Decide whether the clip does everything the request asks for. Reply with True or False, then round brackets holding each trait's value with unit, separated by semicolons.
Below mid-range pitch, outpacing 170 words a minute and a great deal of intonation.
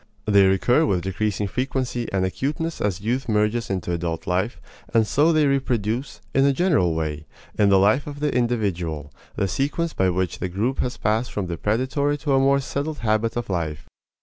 True (110 Hz; 190 wpm; 6.2 semitones)